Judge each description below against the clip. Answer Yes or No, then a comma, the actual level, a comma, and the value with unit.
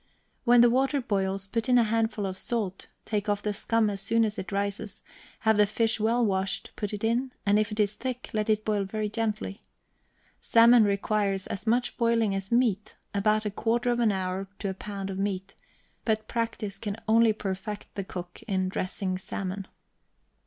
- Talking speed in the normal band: Yes, average, 190 wpm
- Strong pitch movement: No, narrow, 2.6 semitones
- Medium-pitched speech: No, high, 210 Hz